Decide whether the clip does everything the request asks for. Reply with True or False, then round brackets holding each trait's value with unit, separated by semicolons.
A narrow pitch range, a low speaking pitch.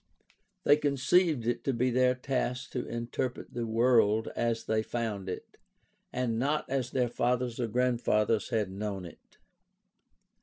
True (2.2 semitones; 120 Hz)